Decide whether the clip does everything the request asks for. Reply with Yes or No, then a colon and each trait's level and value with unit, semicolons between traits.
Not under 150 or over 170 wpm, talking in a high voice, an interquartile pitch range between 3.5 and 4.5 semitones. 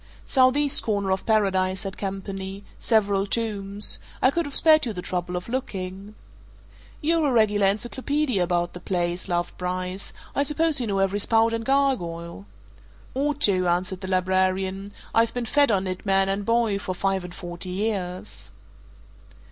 Yes: average, 160 wpm; high, 195 Hz; average, 3.9 semitones